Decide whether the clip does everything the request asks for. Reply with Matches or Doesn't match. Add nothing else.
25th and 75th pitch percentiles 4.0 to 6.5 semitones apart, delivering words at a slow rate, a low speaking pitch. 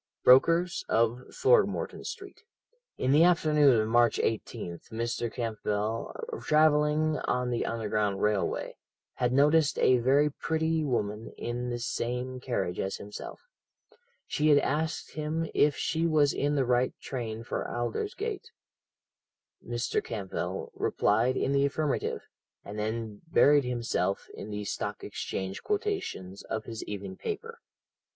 Matches